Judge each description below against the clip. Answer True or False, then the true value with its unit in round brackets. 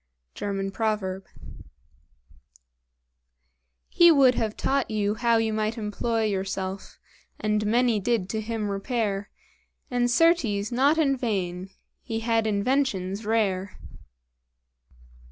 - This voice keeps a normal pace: False (105 wpm)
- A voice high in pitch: True (220 Hz)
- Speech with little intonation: False (3.2 semitones)